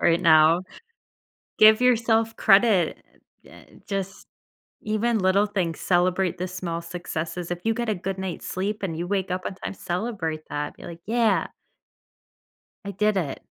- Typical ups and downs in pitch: Yes, average, 3.6 semitones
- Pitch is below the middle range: No, high, 190 Hz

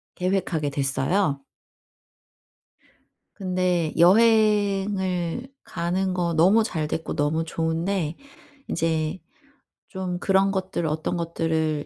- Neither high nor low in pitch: Yes, medium, 175 Hz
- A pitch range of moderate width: Yes, average, 3.1 semitones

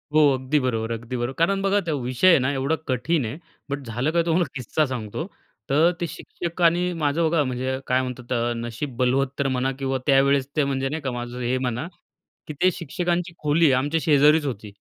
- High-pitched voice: No, medium, 140 Hz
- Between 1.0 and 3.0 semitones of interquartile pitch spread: No, average, 4.1 semitones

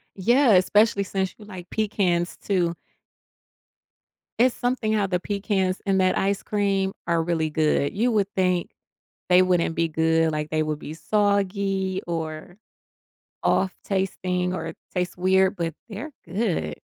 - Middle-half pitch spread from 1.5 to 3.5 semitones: Yes, average, 2.8 semitones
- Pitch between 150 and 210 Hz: Yes, medium, 185 Hz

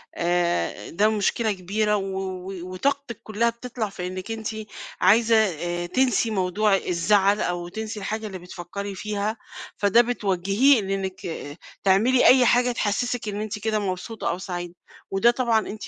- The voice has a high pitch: Yes, high, 210 Hz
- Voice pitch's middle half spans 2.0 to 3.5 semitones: Yes, average, 3.2 semitones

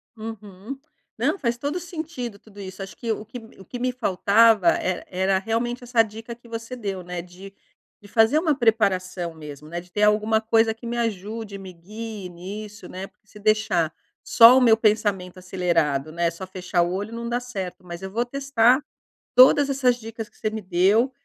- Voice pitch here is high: Yes, high, 215 Hz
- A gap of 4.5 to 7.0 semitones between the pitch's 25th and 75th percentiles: No, average, 4.0 semitones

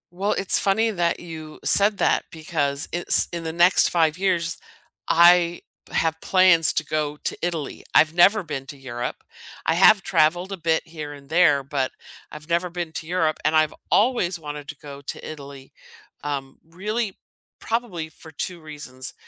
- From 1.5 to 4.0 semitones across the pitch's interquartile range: Yes, average, 3.1 semitones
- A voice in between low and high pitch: Yes, medium, 165 Hz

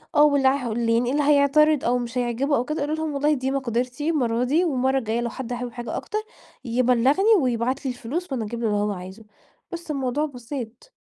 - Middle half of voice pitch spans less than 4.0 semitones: Yes, average, 3.6 semitones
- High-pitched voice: Yes, very high, 255 Hz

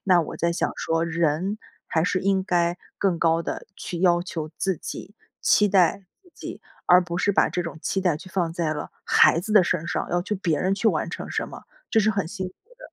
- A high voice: No, medium, 180 Hz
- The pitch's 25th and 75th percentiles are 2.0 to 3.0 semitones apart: Yes, narrow, 2.6 semitones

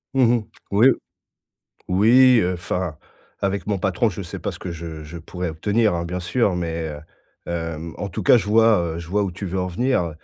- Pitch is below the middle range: Yes, very low, 90 Hz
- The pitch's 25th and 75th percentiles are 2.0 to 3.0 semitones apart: No, average, 3.6 semitones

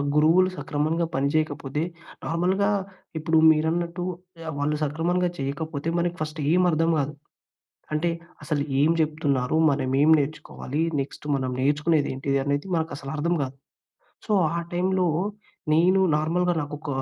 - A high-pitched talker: No, medium, 155 Hz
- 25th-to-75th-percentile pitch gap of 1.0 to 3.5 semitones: Yes, average, 2.8 semitones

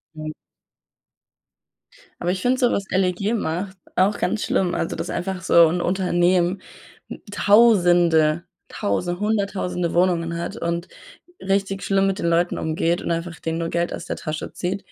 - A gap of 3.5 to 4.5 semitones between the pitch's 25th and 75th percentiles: No, narrow, 2.5 semitones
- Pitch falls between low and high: Yes, medium, 180 Hz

